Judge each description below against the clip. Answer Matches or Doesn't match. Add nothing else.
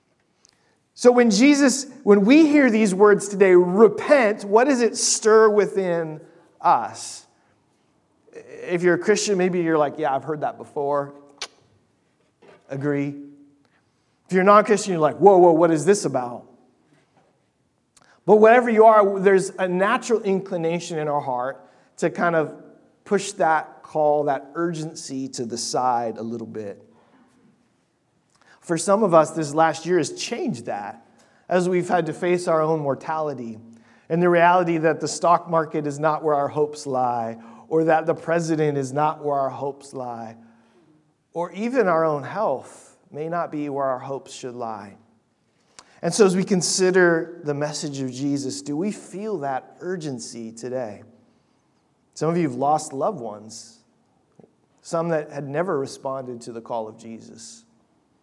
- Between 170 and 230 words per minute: Doesn't match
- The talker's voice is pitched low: Doesn't match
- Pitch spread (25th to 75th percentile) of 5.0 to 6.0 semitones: Matches